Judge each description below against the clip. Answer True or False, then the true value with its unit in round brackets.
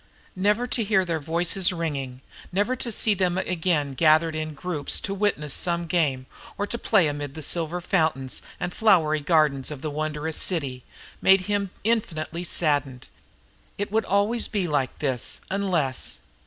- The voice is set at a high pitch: False (165 Hz)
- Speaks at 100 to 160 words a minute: True (155 wpm)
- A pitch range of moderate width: True (4.6 semitones)